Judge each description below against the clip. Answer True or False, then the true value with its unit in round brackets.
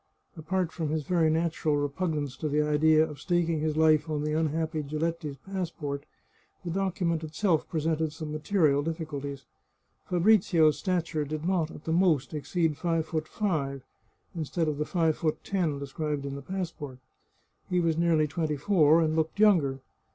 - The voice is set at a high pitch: False (160 Hz)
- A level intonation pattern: True (2.1 semitones)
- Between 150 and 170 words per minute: True (165 wpm)